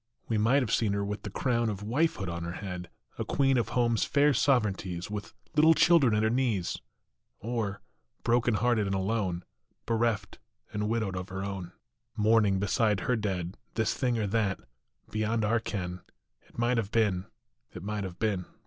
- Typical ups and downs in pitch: Yes, average, 3.3 semitones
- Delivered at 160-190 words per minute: Yes, average, 180 wpm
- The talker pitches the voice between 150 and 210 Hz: No, low, 105 Hz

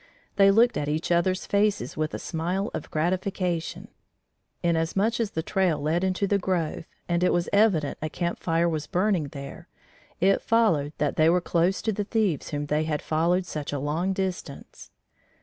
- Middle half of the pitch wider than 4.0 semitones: No, average, 3.7 semitones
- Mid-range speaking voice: Yes, medium, 175 Hz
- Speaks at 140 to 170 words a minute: No, average, 180 wpm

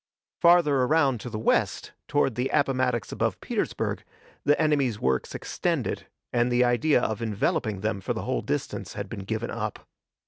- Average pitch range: Yes, average, 4.4 semitones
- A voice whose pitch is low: Yes, low, 120 Hz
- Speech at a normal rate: Yes, average, 165 wpm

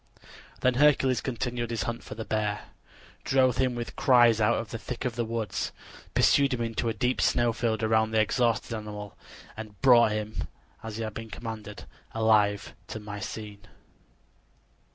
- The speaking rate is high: No, average, 165 wpm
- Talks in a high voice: No, low, 115 Hz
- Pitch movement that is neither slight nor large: No, narrow, 2.0 semitones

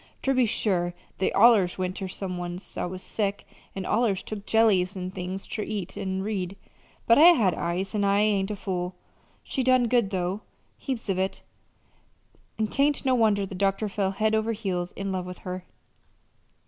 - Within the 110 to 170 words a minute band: No, average, 185 wpm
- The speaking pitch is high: Yes, high, 195 Hz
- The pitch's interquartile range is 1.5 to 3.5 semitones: Yes, average, 2.8 semitones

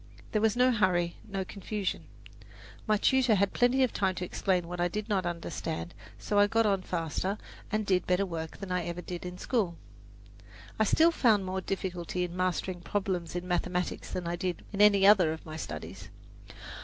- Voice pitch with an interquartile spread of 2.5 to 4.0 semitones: Yes, average, 2.8 semitones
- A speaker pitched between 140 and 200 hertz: Yes, medium, 185 Hz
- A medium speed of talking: Yes, average, 190 wpm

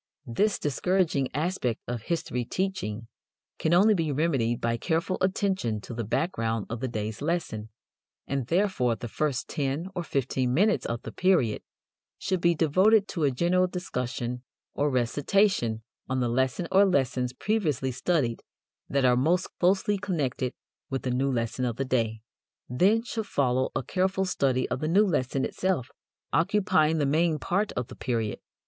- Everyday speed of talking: Yes, average, 160 wpm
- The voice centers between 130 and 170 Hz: Yes, medium, 140 Hz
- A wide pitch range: Yes, wide, 6.8 semitones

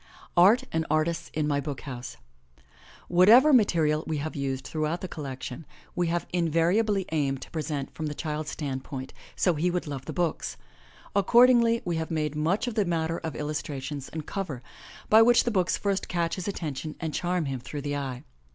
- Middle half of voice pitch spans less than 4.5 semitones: Yes, average, 3.7 semitones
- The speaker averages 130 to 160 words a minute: No, average, 185 wpm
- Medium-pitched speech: Yes, medium, 160 Hz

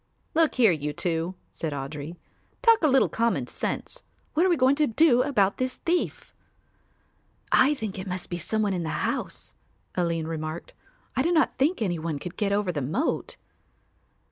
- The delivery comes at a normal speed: Yes, average, 180 wpm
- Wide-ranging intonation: Yes, wide, 8.5 semitones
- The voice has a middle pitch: No, high, 200 Hz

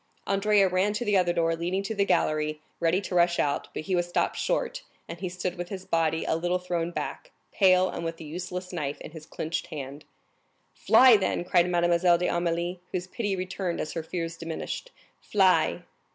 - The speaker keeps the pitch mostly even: Yes, narrow, 2.1 semitones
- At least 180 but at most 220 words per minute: Yes, average, 195 wpm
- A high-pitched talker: No, medium, 175 Hz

